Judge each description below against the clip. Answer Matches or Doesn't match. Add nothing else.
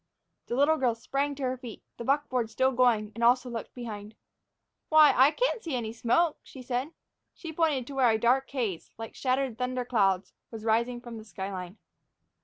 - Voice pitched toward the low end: Doesn't match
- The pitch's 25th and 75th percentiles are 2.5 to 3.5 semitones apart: Matches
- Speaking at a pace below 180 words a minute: Doesn't match